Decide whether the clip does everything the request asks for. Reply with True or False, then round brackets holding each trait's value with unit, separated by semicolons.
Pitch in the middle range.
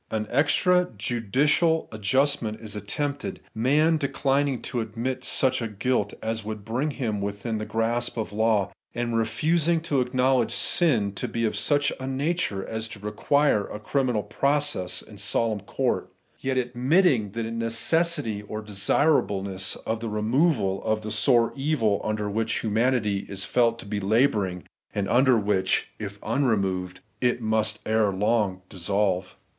False (115 Hz)